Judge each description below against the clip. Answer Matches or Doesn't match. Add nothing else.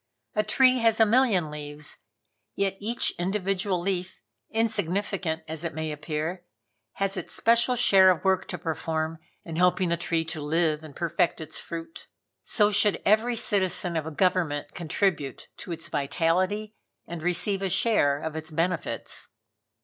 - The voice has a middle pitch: Matches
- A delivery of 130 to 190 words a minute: Matches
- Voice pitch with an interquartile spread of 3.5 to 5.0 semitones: Matches